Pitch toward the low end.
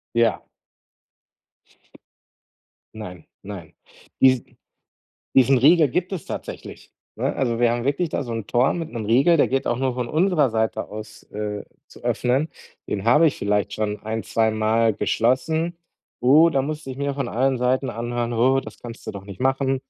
Yes: low, 125 Hz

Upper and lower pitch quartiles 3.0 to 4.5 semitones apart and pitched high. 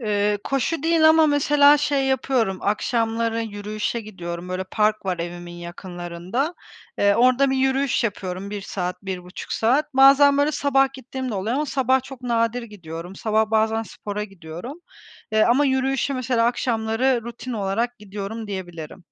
No: average, 5.3 semitones; high, 225 Hz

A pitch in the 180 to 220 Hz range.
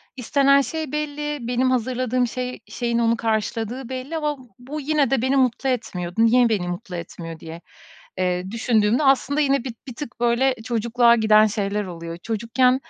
No: high, 240 Hz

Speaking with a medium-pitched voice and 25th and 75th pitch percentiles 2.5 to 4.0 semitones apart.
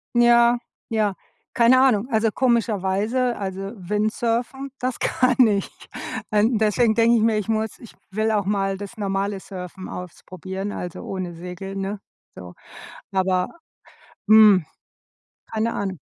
No: high, 210 Hz; average, 3.2 semitones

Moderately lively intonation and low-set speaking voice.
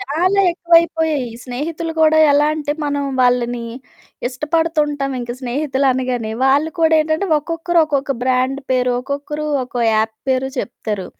No: average, 3.8 semitones; very high, 285 Hz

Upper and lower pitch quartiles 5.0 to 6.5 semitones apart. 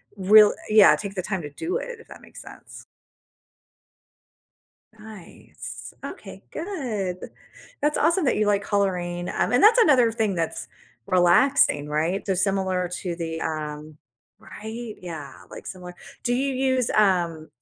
Yes: wide, 5.6 semitones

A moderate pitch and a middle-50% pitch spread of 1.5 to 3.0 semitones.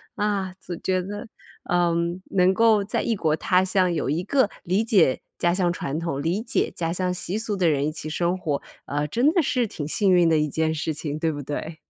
No: medium, 175 Hz; average, 3.7 semitones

